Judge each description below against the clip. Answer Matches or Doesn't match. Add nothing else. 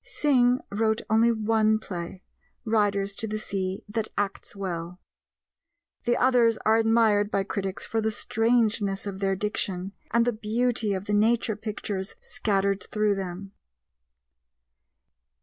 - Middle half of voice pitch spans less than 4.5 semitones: Matches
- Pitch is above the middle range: Matches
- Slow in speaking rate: Matches